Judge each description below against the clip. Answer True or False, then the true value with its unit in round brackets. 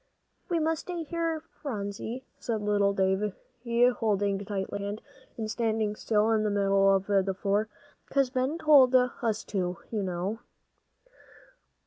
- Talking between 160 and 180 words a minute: False (145 wpm)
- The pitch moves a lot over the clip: False (4.1 semitones)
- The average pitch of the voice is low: False (210 Hz)